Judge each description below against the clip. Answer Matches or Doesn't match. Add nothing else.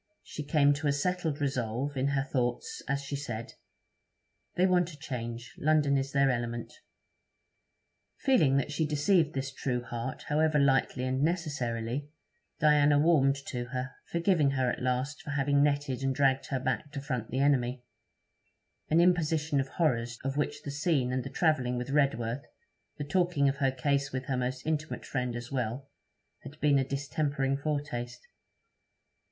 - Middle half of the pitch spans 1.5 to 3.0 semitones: Matches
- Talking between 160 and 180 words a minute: Matches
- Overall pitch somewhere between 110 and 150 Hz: Matches